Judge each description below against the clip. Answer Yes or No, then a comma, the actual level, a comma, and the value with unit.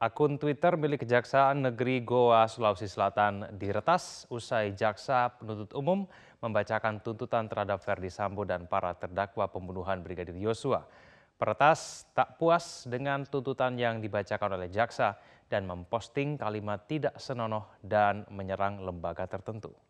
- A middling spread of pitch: Yes, average, 4.2 semitones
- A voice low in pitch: Yes, low, 110 Hz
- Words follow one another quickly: No, average, 125 wpm